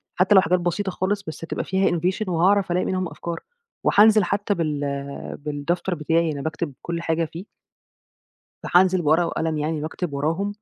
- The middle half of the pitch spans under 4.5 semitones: Yes, average, 2.9 semitones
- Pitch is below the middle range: No, medium, 170 Hz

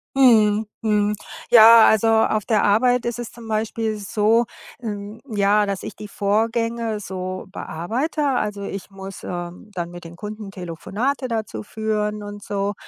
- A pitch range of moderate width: No, narrow, 2.3 semitones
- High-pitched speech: Yes, high, 210 Hz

